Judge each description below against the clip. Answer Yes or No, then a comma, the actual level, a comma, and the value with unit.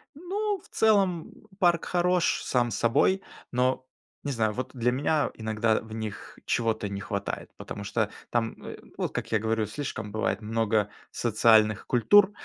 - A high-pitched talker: No, low, 115 Hz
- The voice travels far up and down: Yes, wide, 6.7 semitones